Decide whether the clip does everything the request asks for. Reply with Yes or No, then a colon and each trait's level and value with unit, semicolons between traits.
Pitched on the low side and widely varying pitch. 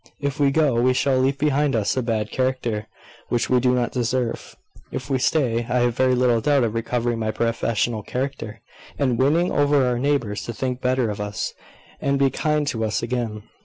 No: low, 125 Hz; average, 3.0 semitones